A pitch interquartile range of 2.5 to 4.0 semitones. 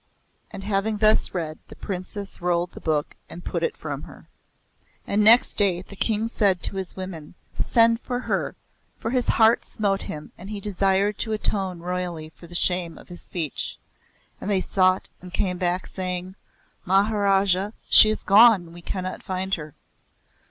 Yes: average, 2.8 semitones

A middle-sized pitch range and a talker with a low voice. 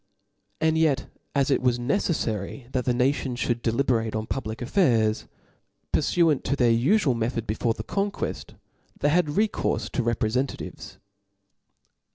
Yes: average, 4.2 semitones; low, 125 Hz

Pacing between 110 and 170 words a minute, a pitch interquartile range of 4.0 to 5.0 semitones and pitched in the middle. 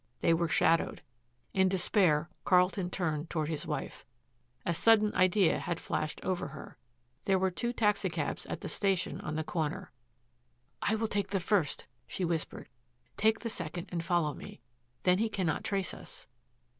No: average, 160 wpm; average, 3.3 semitones; medium, 180 Hz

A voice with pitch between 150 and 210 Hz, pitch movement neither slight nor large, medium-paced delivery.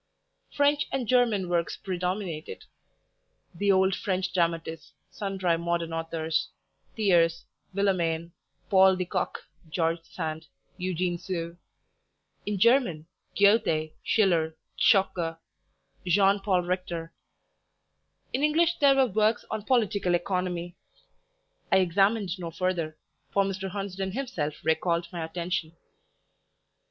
No: medium, 185 Hz; average, 3.1 semitones; slow, 105 wpm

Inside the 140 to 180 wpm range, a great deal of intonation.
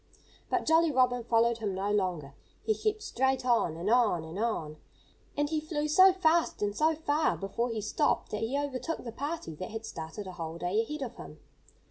No: average, 200 wpm; wide, 7.4 semitones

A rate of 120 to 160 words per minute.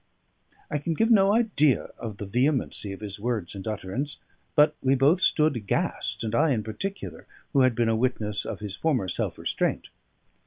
No: average, 185 wpm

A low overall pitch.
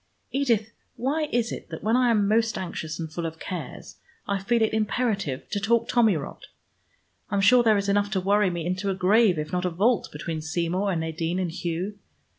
No: high, 200 Hz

